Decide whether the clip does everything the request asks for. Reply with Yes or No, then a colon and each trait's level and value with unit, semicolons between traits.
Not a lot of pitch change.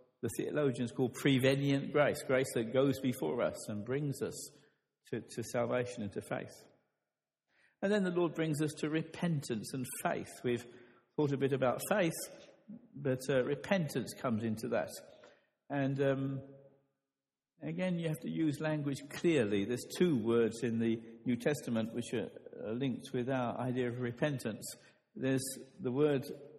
No: average, 3.2 semitones